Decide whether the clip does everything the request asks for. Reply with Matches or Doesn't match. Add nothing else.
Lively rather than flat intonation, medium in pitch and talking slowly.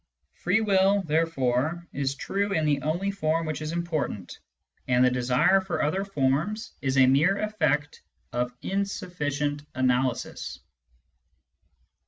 Matches